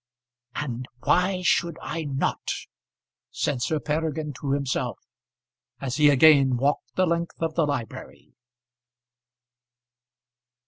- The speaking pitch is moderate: Yes, medium, 150 Hz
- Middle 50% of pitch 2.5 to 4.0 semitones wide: Yes, average, 3.0 semitones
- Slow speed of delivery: Yes, slow, 105 wpm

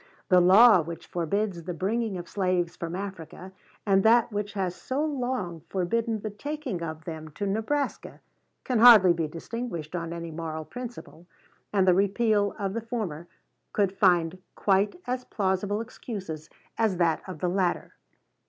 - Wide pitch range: No, average, 4.4 semitones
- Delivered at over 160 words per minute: No, average, 155 wpm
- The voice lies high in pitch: Yes, high, 195 Hz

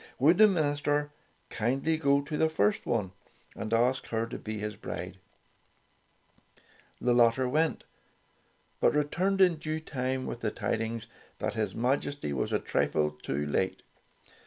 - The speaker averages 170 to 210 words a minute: No, average, 145 wpm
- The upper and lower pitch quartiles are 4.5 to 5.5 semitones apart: Yes, average, 5.1 semitones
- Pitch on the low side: Yes, low, 130 Hz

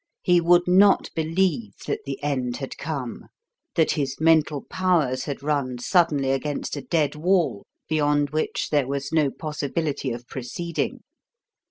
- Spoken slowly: No, average, 145 wpm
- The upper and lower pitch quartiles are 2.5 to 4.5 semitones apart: Yes, average, 3.3 semitones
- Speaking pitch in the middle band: Yes, medium, 150 Hz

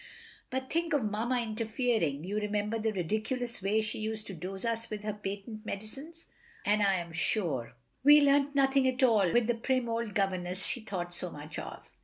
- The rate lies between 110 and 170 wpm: No, average, 190 wpm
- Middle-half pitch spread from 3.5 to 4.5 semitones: Yes, average, 4.0 semitones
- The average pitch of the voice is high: Yes, high, 215 Hz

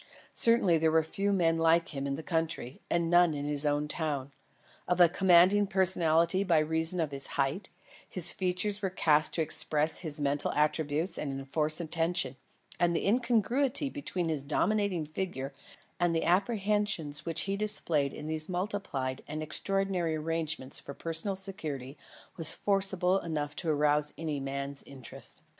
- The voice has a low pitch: No, medium, 165 Hz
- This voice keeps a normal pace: Yes, average, 165 wpm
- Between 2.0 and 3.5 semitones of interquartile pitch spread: No, average, 4.1 semitones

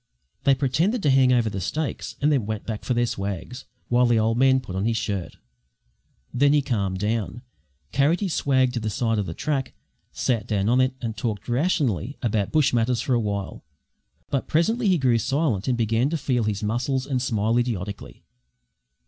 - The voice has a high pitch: No, low, 120 Hz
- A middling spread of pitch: Yes, average, 3.9 semitones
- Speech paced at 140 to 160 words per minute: No, average, 195 wpm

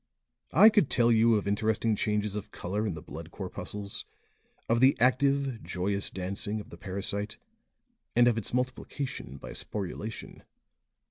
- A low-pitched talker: Yes, low, 105 Hz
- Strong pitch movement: No, average, 3.3 semitones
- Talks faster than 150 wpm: No, average, 145 wpm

